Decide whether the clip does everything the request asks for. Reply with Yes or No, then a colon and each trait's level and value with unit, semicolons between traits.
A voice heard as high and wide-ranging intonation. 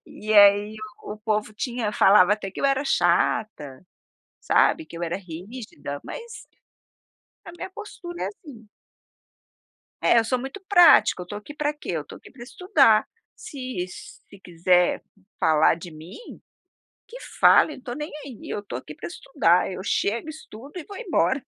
Yes: high, 215 Hz; wide, 7.7 semitones